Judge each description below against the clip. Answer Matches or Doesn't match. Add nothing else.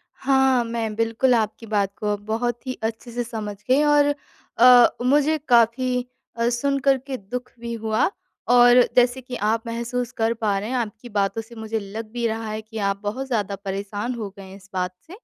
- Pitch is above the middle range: Matches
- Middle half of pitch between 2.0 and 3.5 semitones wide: Matches